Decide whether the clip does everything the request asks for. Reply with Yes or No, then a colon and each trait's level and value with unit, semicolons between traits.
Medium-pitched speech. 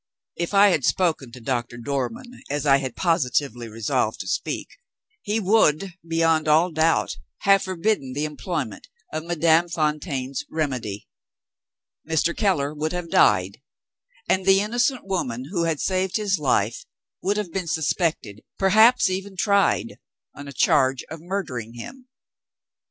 Yes: medium, 160 Hz